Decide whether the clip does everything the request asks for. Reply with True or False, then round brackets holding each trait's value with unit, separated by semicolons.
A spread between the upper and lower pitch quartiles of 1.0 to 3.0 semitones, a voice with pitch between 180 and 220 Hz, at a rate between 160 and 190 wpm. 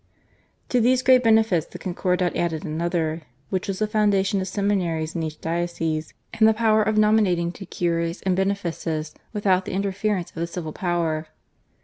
False (3.8 semitones; 185 Hz; 165 wpm)